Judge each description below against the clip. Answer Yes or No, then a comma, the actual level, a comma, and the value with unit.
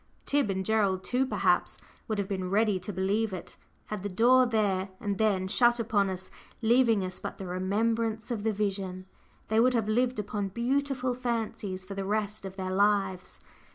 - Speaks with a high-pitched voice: Yes, high, 210 Hz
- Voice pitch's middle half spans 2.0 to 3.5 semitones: Yes, average, 3.2 semitones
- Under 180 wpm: No, average, 185 wpm